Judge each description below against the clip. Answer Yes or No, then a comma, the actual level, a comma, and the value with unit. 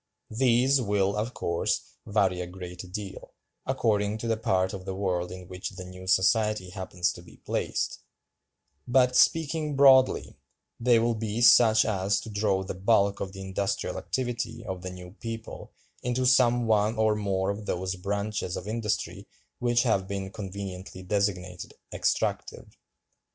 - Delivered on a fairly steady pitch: No, average, 3.4 semitones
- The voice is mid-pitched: No, low, 100 Hz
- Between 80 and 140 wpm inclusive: No, average, 155 wpm